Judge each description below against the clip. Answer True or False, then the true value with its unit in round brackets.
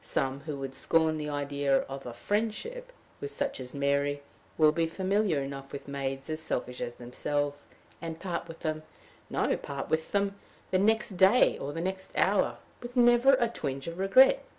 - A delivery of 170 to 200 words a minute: True (180 wpm)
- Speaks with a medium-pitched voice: True (155 Hz)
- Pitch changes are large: True (6.1 semitones)